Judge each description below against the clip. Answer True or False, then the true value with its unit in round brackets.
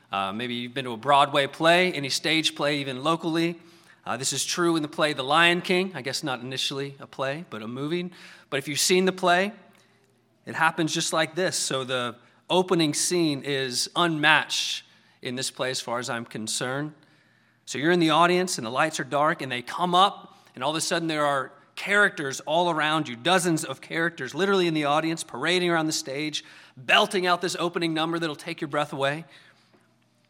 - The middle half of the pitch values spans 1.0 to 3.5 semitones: False (4.3 semitones)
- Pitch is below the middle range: False (155 Hz)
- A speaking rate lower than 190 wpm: False (205 wpm)